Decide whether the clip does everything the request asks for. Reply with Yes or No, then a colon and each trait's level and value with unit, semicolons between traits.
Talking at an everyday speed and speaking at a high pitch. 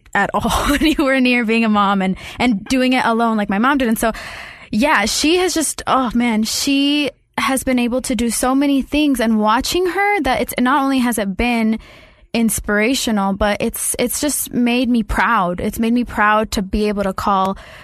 No: fast, 210 wpm; high, 240 Hz